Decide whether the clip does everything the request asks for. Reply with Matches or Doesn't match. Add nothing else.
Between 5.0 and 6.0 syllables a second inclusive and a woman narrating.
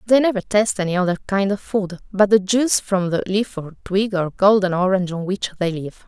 Matches